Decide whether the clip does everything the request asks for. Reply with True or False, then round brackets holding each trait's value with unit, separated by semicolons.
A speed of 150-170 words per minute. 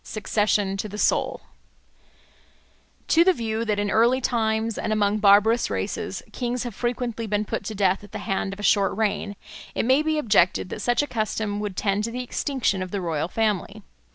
False (195 wpm)